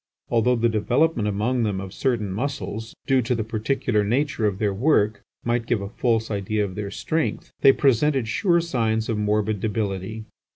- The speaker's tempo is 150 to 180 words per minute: Yes, average, 175 wpm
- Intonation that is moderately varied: Yes, average, 3.1 semitones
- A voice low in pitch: Yes, low, 110 Hz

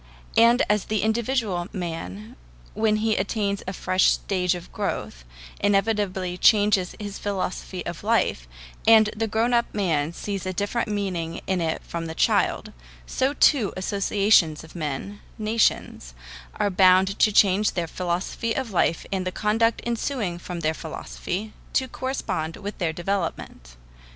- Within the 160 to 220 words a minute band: No, average, 145 wpm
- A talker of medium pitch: No, high, 195 Hz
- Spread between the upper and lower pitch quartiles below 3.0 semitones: No, average, 3.7 semitones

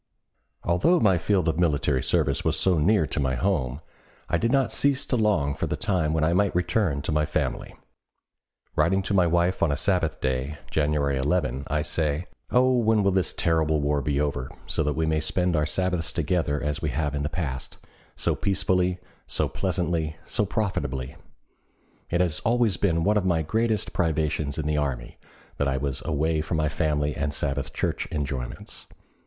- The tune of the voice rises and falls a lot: No, average, 4.1 semitones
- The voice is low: Yes, very low, 80 Hz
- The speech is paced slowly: No, average, 185 wpm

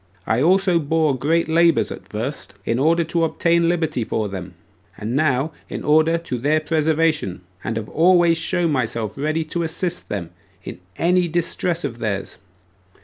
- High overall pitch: No, medium, 155 Hz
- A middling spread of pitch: No, wide, 5.8 semitones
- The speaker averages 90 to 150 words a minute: No, average, 160 wpm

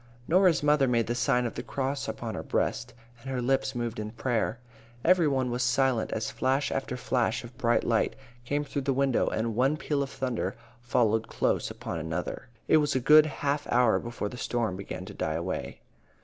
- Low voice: Yes, low, 125 Hz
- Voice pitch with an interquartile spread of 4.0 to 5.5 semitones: No, average, 3.0 semitones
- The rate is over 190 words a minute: Yes, average, 200 wpm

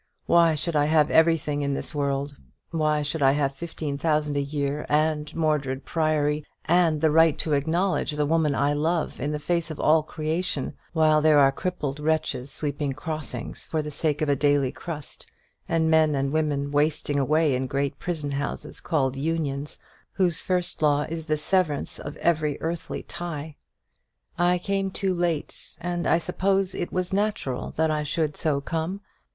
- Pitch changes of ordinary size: No, narrow, 2.3 semitones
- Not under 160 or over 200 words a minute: Yes, average, 175 wpm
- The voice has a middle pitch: Yes, medium, 155 Hz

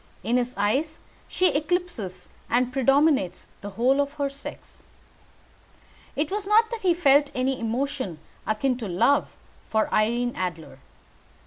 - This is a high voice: Yes, very high, 265 Hz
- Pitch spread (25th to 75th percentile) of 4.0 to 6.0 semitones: Yes, average, 5.2 semitones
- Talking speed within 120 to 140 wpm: Yes, slow, 135 wpm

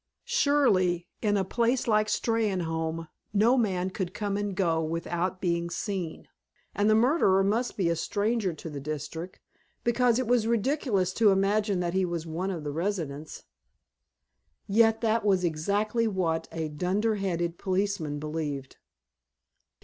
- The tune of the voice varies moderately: Yes, average, 4.4 semitones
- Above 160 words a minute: No, average, 140 wpm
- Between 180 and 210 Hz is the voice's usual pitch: Yes, high, 190 Hz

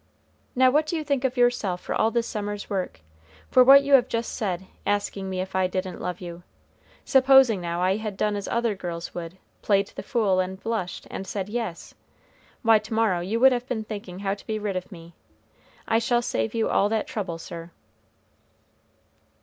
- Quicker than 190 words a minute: Yes, average, 200 wpm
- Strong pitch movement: No, average, 4.0 semitones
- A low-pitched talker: No, high, 205 Hz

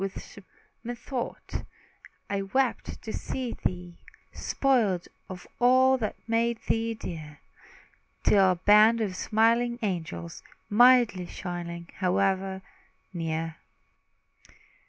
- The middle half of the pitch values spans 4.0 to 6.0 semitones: Yes, average, 4.6 semitones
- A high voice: Yes, high, 200 Hz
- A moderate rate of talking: No, slow, 95 wpm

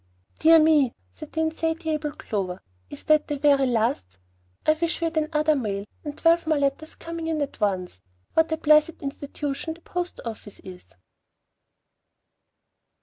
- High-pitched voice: Yes, very high, 300 Hz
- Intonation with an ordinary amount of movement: Yes, average, 5.0 semitones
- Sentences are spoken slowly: No, average, 150 wpm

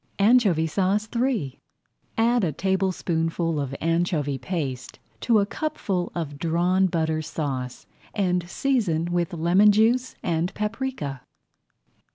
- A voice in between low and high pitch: Yes, medium, 175 Hz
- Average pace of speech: No, slow, 115 wpm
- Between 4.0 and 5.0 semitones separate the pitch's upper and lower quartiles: Yes, average, 4.6 semitones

